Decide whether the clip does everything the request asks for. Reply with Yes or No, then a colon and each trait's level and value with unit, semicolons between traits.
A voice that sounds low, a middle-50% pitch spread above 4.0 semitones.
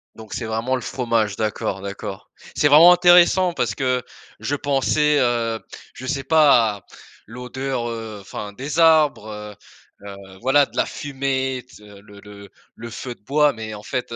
Yes: low, 125 Hz; average, 4.8 semitones